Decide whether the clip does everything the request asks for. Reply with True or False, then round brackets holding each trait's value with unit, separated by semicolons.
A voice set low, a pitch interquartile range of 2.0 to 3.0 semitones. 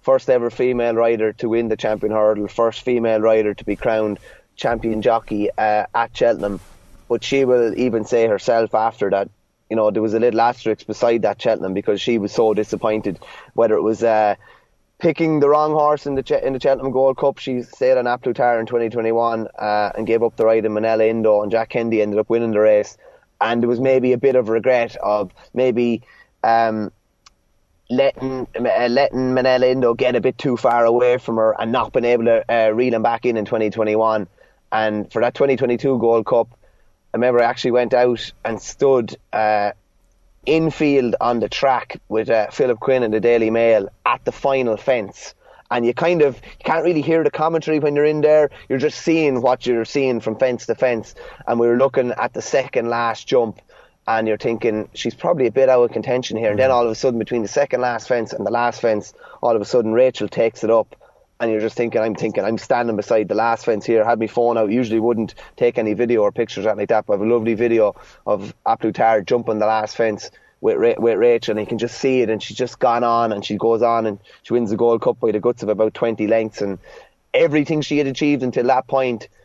True (115 Hz; 2.7 semitones)